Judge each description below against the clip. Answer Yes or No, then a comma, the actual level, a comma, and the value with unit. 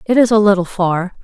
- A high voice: Yes, high, 200 Hz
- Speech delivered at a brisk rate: Yes, fast, 245 wpm